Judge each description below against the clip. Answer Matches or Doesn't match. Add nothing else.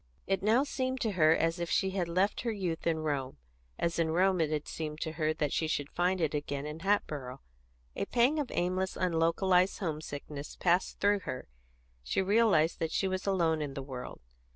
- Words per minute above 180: Matches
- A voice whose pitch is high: Doesn't match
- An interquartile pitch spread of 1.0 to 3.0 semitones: Doesn't match